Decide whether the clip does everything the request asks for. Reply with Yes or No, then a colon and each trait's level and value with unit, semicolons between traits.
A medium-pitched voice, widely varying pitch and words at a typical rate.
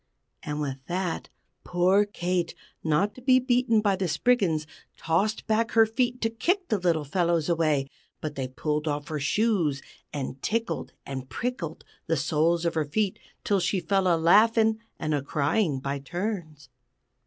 Yes: medium, 175 Hz; wide, 6.2 semitones; average, 165 wpm